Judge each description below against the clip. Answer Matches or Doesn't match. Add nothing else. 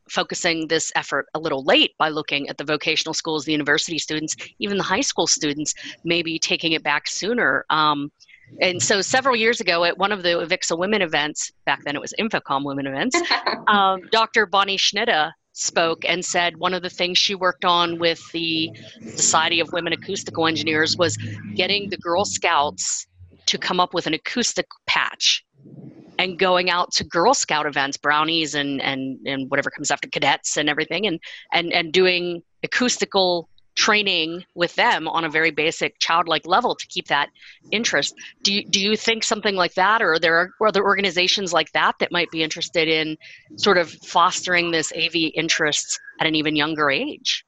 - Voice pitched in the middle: Matches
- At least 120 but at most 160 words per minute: Doesn't match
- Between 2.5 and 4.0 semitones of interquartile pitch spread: Matches